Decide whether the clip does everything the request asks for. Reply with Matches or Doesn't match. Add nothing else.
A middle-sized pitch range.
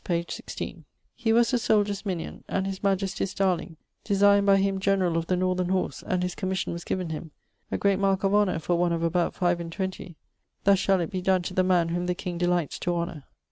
Doesn't match